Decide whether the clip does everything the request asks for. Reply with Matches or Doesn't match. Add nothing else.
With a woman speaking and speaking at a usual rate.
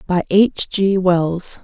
Matches